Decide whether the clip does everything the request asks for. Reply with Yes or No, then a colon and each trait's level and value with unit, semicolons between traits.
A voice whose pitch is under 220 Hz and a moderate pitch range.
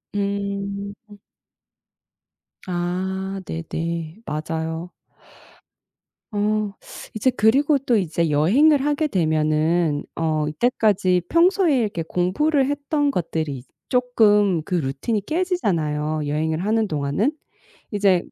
No: high, 190 Hz; wide, 6.3 semitones